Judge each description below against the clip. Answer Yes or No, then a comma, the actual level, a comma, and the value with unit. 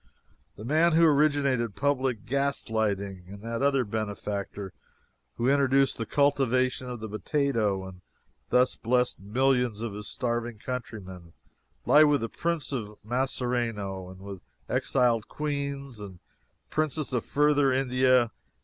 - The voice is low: Yes, low, 125 Hz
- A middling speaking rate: No, slow, 130 wpm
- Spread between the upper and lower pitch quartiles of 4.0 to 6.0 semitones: Yes, average, 4.7 semitones